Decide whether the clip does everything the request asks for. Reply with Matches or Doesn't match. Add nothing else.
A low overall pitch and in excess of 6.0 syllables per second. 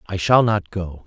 Doesn't match